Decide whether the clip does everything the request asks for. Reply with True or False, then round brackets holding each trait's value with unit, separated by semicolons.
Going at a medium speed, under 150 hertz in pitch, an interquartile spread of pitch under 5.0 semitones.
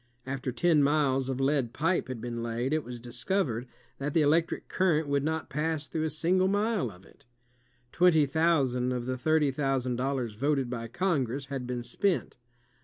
True (180 wpm; 140 Hz; 4.2 semitones)